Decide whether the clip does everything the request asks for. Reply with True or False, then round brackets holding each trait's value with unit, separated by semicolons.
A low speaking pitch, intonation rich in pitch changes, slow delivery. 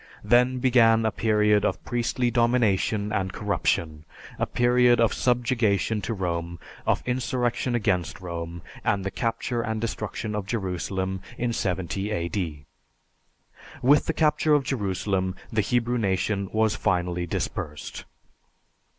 False (105 Hz; 4.3 semitones; 125 wpm)